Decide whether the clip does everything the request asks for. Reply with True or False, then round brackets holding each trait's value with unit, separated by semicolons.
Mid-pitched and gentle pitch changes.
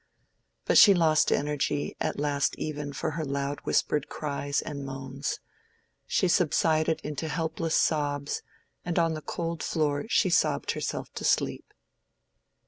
True (150 Hz; 2.2 semitones)